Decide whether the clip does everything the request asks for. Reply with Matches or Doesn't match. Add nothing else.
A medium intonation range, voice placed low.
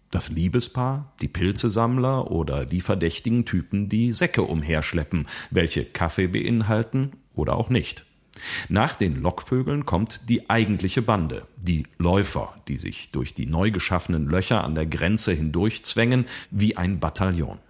Doesn't match